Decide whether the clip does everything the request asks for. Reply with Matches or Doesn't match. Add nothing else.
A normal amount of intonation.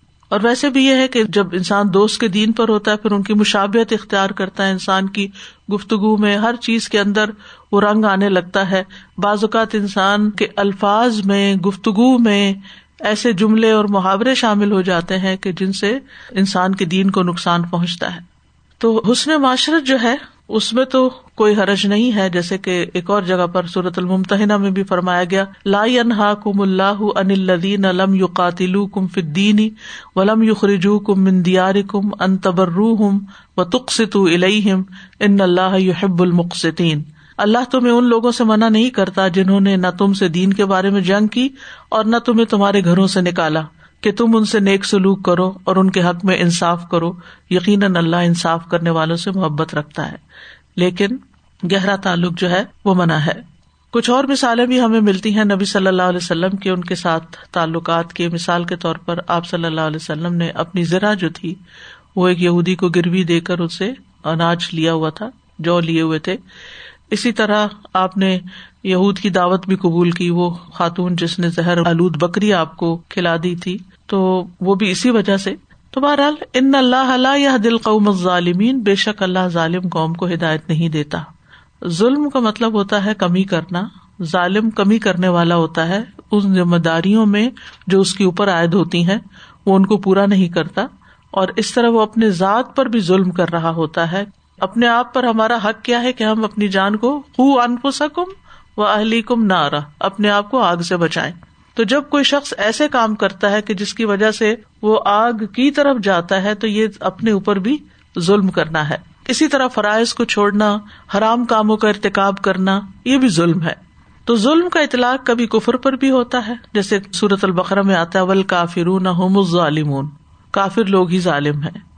Matches